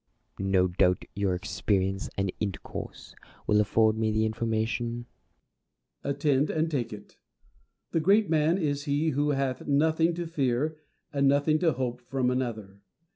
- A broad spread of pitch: Yes, wide, 5.7 semitones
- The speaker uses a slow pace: No, average, 150 wpm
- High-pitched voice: No, low, 130 Hz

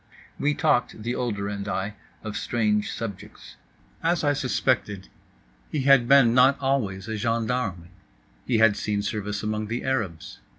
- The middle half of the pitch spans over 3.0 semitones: Yes, average, 3.7 semitones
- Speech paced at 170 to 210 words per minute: No, average, 145 wpm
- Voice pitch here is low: Yes, low, 110 Hz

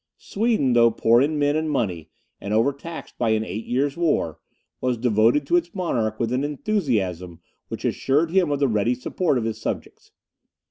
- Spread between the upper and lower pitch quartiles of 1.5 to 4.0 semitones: No, average, 5.3 semitones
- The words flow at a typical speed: Yes, average, 180 wpm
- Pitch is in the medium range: No, low, 125 Hz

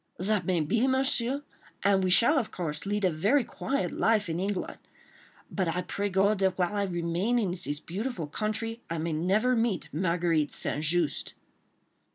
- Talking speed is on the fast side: No, average, 175 wpm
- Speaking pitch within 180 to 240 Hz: Yes, high, 190 Hz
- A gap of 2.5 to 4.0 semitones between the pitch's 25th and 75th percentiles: No, average, 4.6 semitones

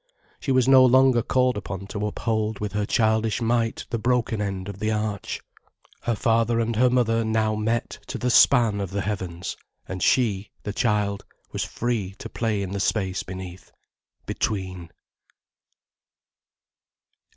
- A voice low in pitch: Yes, low, 110 Hz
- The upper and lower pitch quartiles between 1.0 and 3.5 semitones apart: Yes, average, 2.8 semitones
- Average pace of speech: Yes, average, 150 wpm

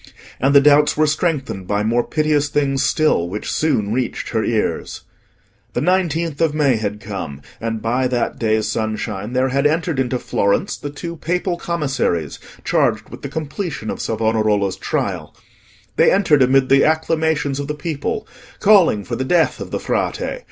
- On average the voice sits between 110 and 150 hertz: Yes, medium, 140 Hz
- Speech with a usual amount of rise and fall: No, wide, 6.1 semitones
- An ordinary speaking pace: Yes, average, 165 wpm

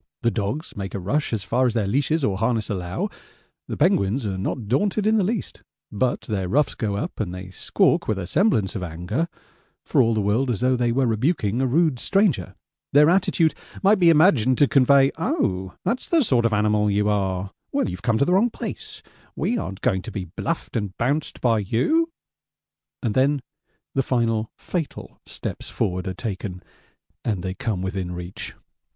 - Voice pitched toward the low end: Yes, low, 115 Hz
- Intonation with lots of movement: Yes, wide, 6.6 semitones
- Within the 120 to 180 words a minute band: No, average, 190 wpm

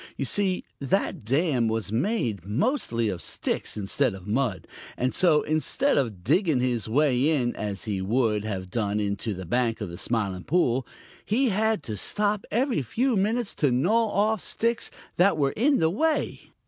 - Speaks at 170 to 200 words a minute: Yes, average, 175 wpm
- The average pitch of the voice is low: Yes, low, 130 Hz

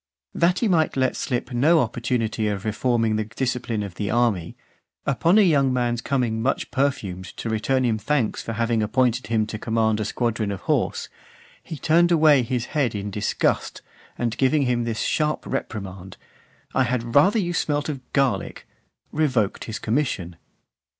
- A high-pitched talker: No, low, 120 Hz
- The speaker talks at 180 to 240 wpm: No, average, 170 wpm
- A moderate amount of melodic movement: Yes, average, 4.1 semitones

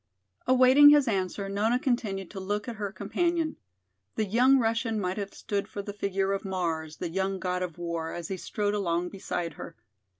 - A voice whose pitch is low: No, high, 200 Hz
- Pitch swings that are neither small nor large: Yes, average, 3.5 semitones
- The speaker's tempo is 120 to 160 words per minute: No, average, 190 wpm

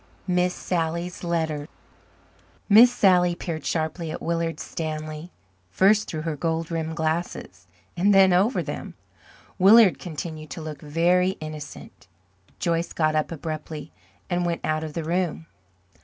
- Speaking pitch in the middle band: Yes, medium, 165 Hz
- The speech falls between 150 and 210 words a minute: No, slow, 135 wpm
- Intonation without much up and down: Yes, narrow, 2.3 semitones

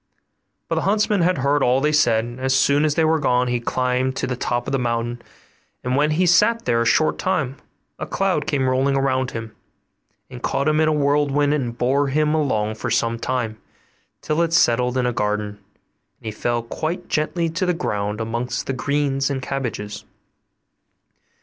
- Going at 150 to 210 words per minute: Yes, average, 195 wpm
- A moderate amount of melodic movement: Yes, average, 4.0 semitones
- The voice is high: No, low, 130 Hz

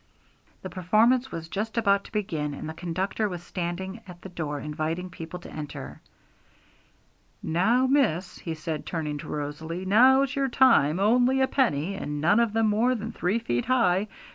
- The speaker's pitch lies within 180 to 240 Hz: Yes, medium, 185 Hz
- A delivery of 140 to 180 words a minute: Yes, average, 170 wpm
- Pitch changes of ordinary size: No, wide, 6.0 semitones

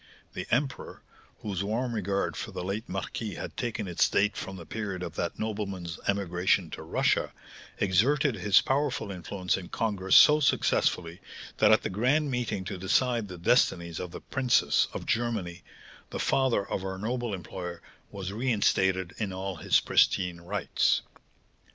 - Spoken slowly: No, average, 155 wpm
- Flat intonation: No, average, 4.1 semitones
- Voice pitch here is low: Yes, low, 100 Hz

